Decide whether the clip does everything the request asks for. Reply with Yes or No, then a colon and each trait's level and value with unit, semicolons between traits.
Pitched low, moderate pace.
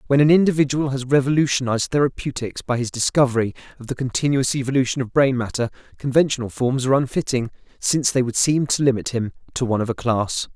Yes: low, 130 Hz; average, 180 wpm